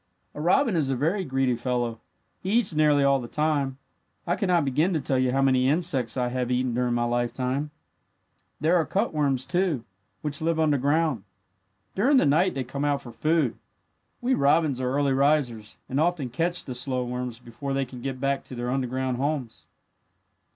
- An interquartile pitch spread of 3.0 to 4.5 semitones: Yes, average, 3.7 semitones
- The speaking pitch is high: No, low, 135 Hz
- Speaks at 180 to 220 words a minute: Yes, average, 185 wpm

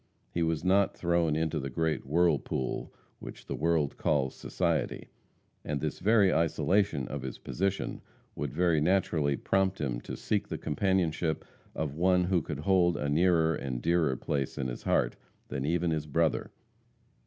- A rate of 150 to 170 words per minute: Yes, average, 160 wpm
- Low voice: Yes, very low, 80 Hz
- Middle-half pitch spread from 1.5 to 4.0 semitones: Yes, average, 3.4 semitones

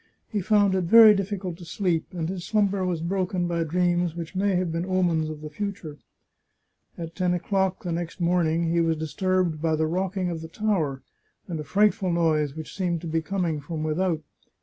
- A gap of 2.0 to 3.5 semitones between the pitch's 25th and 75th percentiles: Yes, narrow, 2.6 semitones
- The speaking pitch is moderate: Yes, medium, 175 Hz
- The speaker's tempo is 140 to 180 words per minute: No, average, 195 wpm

